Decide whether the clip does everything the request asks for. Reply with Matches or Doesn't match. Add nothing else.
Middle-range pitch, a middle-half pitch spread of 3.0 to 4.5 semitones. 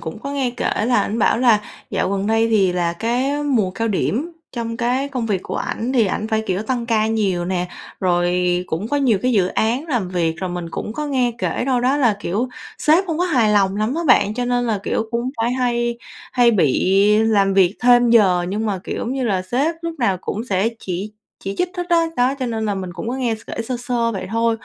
Doesn't match